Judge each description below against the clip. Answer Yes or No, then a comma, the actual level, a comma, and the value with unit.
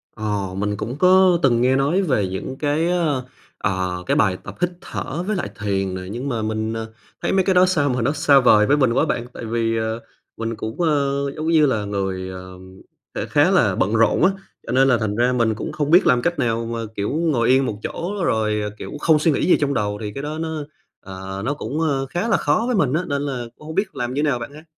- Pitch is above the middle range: No, low, 130 Hz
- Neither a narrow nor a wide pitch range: No, wide, 5.9 semitones